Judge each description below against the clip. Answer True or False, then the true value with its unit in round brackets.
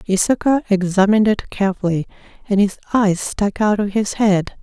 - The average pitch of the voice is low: False (200 Hz)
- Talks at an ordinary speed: True (155 wpm)